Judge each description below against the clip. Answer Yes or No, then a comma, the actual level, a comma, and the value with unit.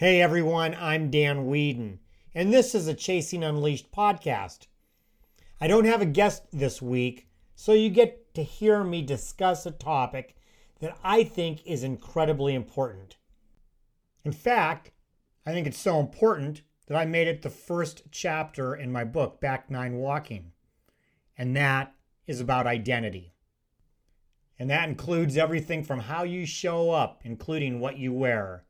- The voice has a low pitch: No, medium, 150 Hz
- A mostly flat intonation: No, average, 4.9 semitones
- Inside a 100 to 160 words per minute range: Yes, average, 150 wpm